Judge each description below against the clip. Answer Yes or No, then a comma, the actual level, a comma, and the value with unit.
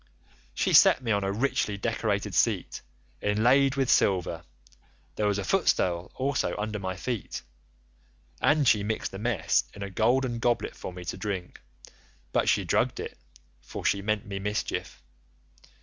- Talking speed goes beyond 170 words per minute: No, average, 155 wpm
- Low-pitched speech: Yes, low, 105 Hz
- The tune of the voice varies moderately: Yes, average, 3.5 semitones